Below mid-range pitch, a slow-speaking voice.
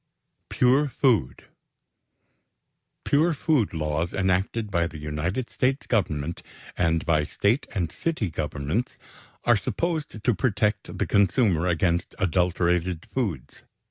Yes: very low, 95 Hz; slow, 110 wpm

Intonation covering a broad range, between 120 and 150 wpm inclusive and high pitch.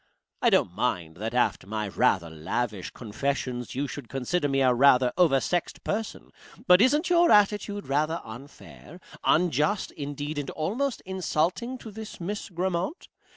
No: wide, 7.7 semitones; average, 145 wpm; medium, 150 Hz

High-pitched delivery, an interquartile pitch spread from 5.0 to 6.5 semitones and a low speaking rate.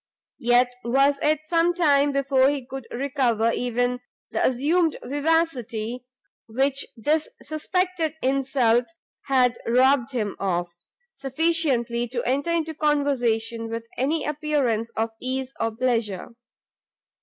No: very high, 265 Hz; average, 3.8 semitones; slow, 115 wpm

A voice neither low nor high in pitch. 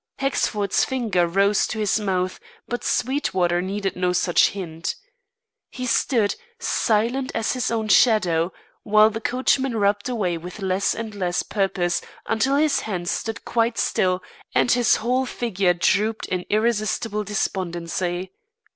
No: high, 210 Hz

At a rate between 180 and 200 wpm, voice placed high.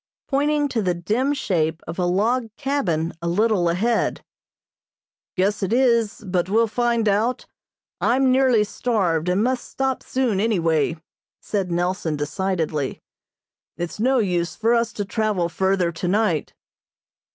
No: average, 140 wpm; high, 205 Hz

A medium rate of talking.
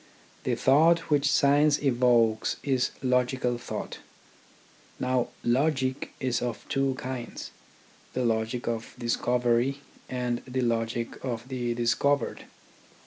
No: slow, 110 wpm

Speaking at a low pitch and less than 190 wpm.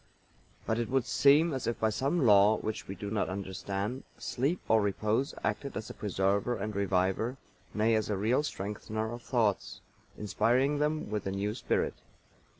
Yes: low, 110 Hz; average, 170 wpm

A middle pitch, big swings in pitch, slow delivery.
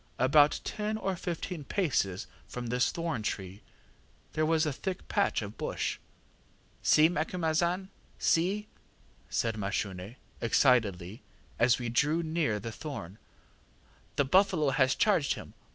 Yes: medium, 145 Hz; wide, 6.9 semitones; slow, 125 wpm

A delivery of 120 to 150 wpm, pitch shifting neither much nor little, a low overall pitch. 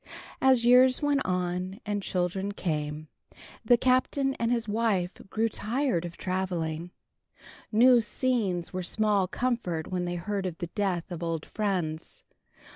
No: slow, 135 wpm; average, 4.9 semitones; high, 195 Hz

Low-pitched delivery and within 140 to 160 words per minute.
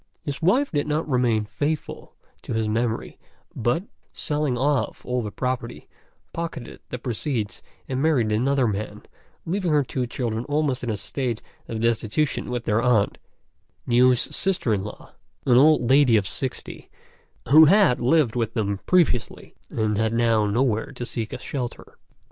Yes: low, 125 Hz; average, 155 wpm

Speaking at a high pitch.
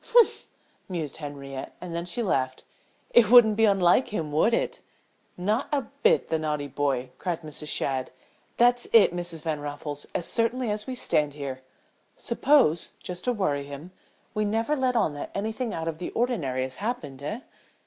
No: medium, 175 Hz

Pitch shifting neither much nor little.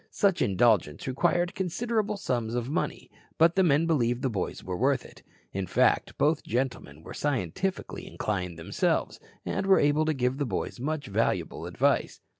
No: wide, 6.8 semitones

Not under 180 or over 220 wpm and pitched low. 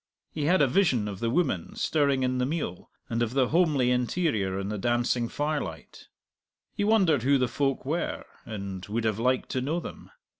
Yes: average, 190 wpm; low, 125 Hz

